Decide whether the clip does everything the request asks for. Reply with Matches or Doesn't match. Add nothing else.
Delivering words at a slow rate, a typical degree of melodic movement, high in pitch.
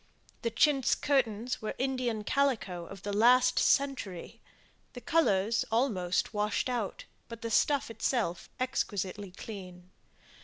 Matches